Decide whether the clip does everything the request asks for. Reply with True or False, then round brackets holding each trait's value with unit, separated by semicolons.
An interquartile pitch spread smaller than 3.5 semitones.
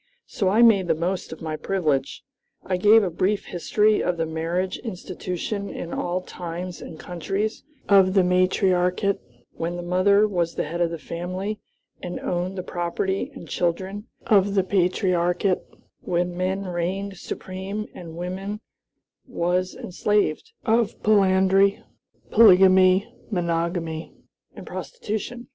True (2.4 semitones)